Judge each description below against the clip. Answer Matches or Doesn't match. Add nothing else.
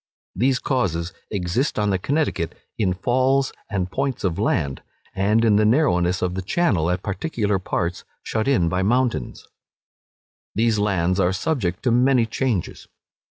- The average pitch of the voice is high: Doesn't match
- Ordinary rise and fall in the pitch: Doesn't match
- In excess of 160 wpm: Doesn't match